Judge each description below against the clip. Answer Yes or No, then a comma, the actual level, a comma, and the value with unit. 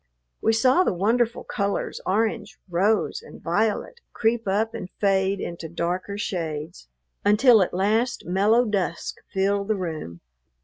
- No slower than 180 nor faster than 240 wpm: No, slow, 135 wpm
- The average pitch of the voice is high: Yes, high, 200 Hz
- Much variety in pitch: No, average, 3.6 semitones